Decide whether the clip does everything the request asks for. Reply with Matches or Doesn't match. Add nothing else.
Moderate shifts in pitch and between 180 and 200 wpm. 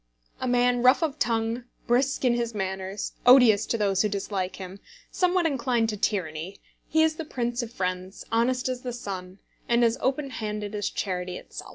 Matches